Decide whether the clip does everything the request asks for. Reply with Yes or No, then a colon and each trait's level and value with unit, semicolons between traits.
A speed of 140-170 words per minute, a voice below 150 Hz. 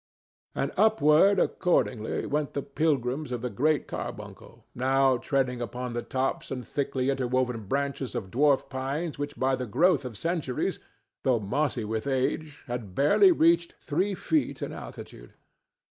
Yes: average, 145 wpm; low, 135 Hz